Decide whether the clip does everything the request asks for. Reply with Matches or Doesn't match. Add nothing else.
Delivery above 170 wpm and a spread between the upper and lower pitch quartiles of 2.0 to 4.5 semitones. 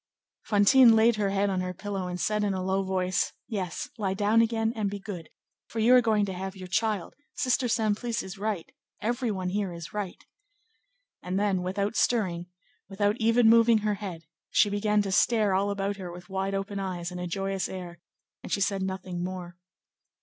Matches